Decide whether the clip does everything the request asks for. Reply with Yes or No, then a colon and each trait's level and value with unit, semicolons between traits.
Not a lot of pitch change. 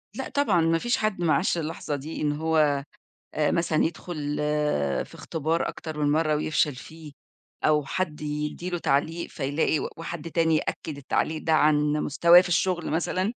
Yes: narrow, 2.1 semitones